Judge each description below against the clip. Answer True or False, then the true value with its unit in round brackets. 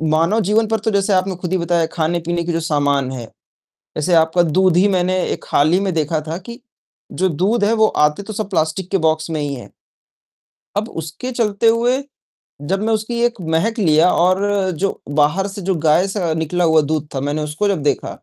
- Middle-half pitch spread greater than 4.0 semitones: True (4.4 semitones)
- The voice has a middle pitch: True (180 Hz)